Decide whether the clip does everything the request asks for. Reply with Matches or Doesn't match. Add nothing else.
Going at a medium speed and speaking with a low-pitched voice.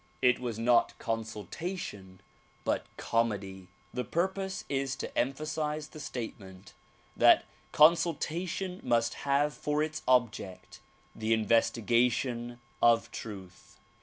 Doesn't match